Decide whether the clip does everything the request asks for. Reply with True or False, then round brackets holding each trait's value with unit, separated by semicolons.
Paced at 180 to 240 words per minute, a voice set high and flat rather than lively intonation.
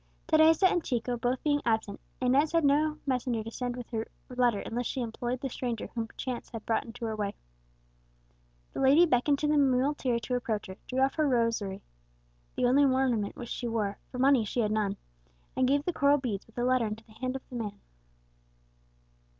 False (200 wpm; 245 Hz; 3.2 semitones)